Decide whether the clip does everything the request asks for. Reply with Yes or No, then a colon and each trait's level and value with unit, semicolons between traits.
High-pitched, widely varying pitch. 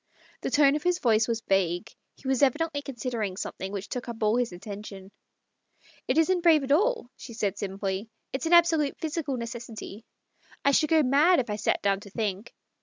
Yes: high, 240 Hz; wide, 6.3 semitones